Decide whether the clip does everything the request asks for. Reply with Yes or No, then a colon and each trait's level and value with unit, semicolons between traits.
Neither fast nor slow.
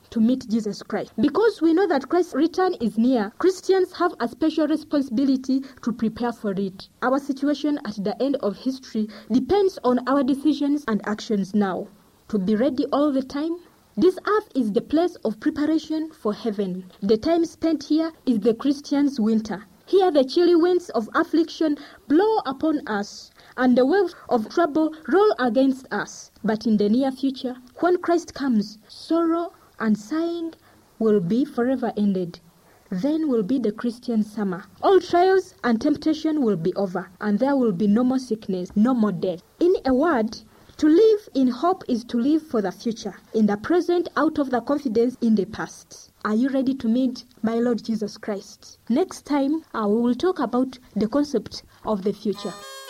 Yes: average, 180 wpm